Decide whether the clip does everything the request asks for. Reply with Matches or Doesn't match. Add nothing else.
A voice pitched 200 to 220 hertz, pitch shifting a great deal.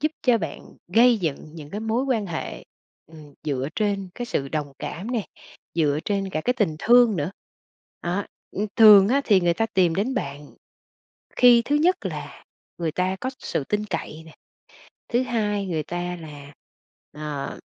Doesn't match